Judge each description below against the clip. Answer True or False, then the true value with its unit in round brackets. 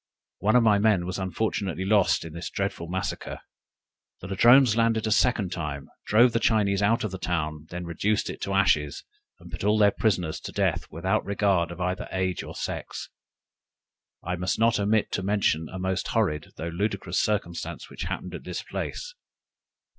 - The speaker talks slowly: False (175 wpm)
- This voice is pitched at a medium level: False (95 Hz)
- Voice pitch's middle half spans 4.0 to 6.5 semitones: False (3.5 semitones)